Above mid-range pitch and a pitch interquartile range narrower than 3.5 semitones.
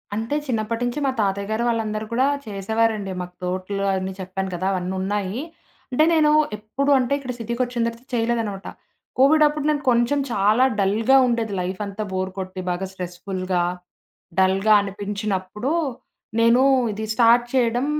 No: high, 215 Hz; average, 3.8 semitones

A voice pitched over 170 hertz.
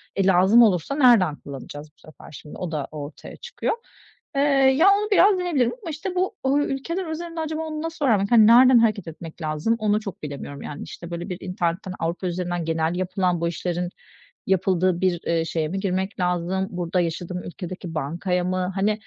Yes: medium, 185 Hz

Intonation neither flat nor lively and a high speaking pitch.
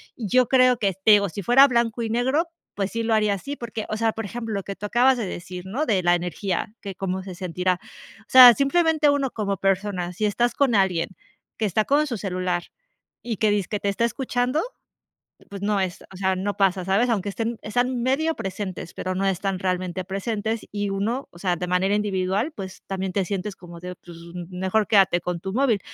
Yes: average, 4.1 semitones; high, 205 Hz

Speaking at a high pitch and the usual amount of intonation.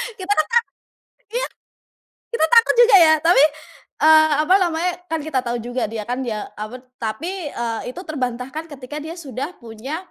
No: very high, 305 Hz; wide, 5.8 semitones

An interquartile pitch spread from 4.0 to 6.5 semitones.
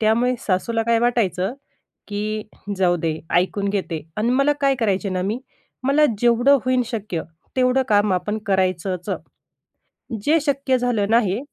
Yes: average, 4.5 semitones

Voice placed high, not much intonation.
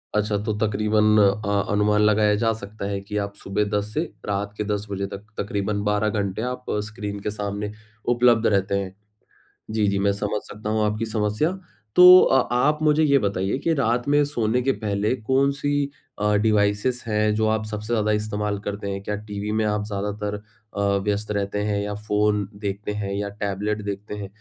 No: low, 105 Hz; narrow, 1.2 semitones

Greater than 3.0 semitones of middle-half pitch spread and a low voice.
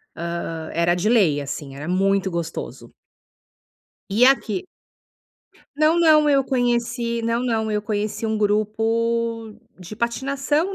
No: average, 4.0 semitones; high, 225 Hz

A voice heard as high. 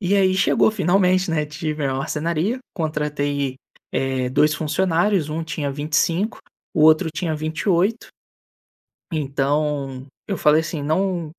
No: medium, 155 Hz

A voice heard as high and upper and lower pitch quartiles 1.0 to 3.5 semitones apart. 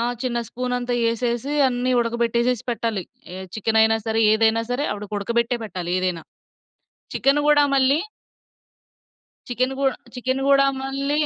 Yes: high, 240 Hz; average, 2.7 semitones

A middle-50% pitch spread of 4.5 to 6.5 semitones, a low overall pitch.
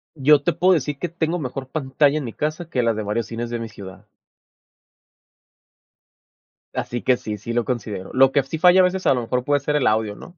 Yes: average, 5.0 semitones; low, 130 Hz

